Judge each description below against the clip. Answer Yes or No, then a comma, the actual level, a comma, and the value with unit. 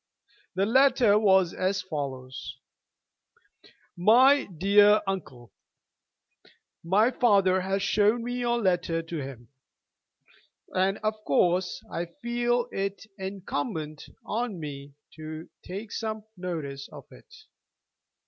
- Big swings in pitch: No, average, 4.7 semitones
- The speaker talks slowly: Yes, slow, 105 wpm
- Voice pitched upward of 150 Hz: Yes, high, 190 Hz